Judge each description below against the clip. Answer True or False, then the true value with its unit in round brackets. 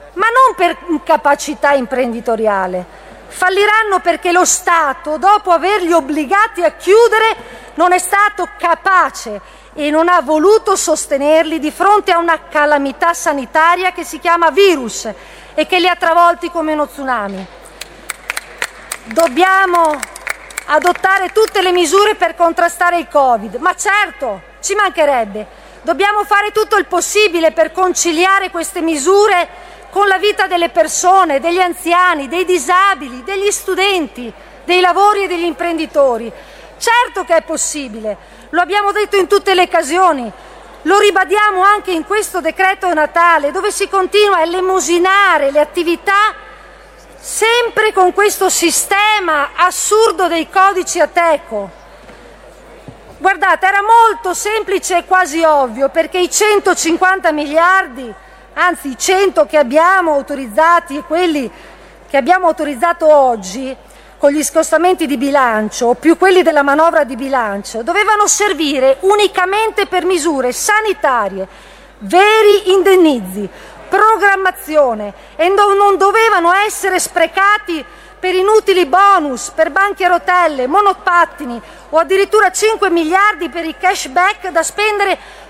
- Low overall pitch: False (350 Hz)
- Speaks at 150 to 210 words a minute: False (125 wpm)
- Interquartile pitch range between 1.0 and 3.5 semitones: False (4.2 semitones)